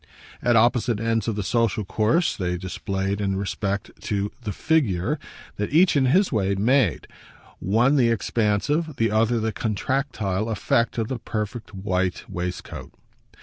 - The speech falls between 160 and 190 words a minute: No, average, 150 wpm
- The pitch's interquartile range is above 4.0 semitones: No, average, 3.6 semitones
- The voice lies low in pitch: Yes, low, 110 Hz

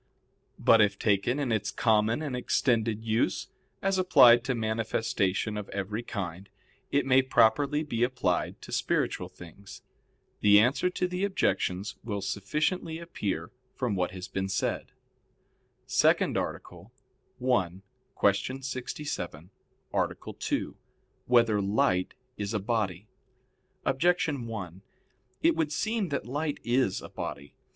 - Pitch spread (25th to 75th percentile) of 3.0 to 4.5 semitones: No, average, 5.3 semitones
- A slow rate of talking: Yes, slow, 130 wpm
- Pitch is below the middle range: Yes, low, 115 Hz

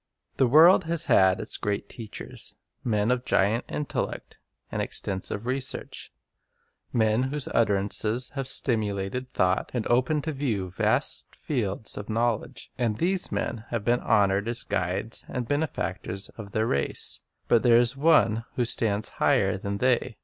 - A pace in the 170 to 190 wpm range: No, average, 150 wpm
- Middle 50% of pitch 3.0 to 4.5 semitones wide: Yes, average, 3.9 semitones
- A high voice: No, low, 115 Hz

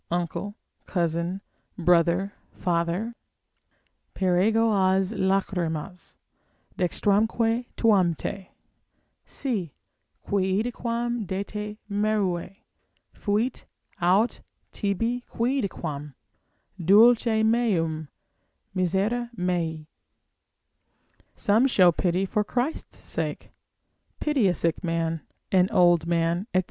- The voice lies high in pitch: Yes, high, 195 Hz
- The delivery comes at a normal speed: No, slow, 85 wpm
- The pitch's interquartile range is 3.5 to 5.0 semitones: Yes, average, 4.1 semitones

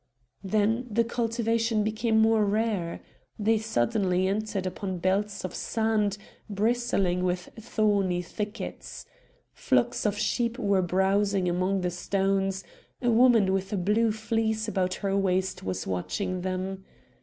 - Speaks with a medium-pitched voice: No, high, 205 Hz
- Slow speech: Yes, slow, 130 wpm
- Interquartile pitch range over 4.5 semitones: No, average, 3.0 semitones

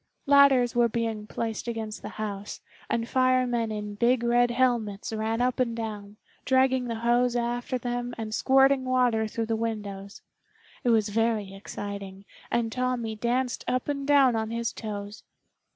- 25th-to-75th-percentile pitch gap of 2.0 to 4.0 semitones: Yes, narrow, 2.5 semitones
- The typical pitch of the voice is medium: No, high, 235 Hz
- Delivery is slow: No, average, 155 wpm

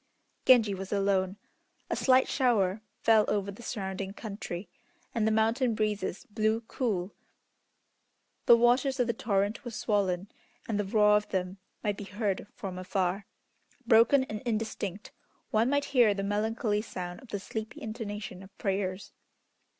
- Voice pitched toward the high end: Yes, high, 210 Hz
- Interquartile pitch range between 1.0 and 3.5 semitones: Yes, narrow, 2.6 semitones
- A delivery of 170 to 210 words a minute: No, average, 150 wpm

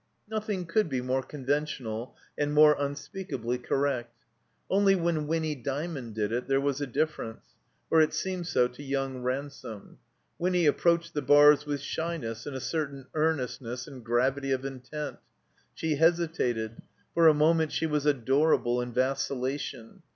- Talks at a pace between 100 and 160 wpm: Yes, average, 150 wpm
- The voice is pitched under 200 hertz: Yes, medium, 140 Hz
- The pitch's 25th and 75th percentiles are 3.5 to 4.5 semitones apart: Yes, average, 4.0 semitones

